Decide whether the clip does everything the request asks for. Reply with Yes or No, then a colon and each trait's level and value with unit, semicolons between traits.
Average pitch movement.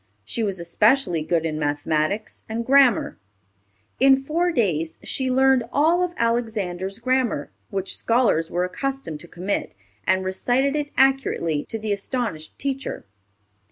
No: wide, 7.3 semitones